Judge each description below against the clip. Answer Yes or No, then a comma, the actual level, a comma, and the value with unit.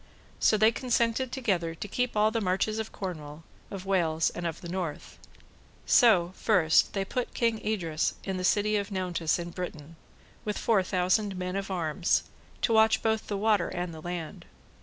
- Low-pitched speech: No, high, 190 Hz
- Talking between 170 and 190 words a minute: Yes, average, 180 wpm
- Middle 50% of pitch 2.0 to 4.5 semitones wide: Yes, average, 4.0 semitones